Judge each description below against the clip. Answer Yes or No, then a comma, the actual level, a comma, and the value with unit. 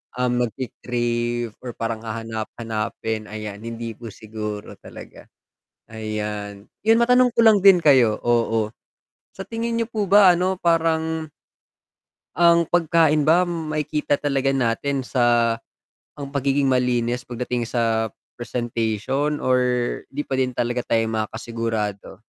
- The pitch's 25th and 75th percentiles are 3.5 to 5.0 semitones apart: No, wide, 5.4 semitones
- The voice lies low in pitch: Yes, low, 125 Hz